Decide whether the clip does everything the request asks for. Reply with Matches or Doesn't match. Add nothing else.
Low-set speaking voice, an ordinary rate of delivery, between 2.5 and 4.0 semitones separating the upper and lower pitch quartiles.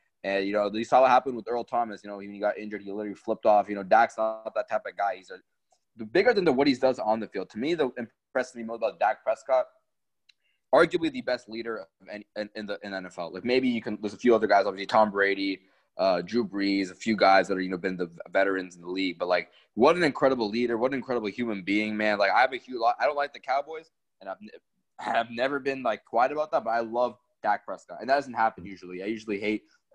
Doesn't match